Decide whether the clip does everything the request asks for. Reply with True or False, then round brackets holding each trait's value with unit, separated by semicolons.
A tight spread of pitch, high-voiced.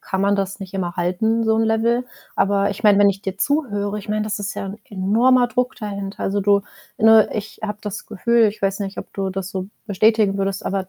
True (2.1 semitones; 205 Hz)